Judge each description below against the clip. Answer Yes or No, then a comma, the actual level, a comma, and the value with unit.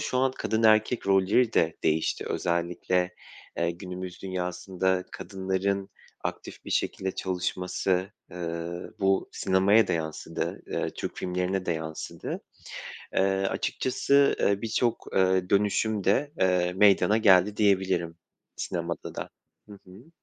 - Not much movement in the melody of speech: Yes, narrow, 2.2 semitones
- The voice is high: No, very low, 95 Hz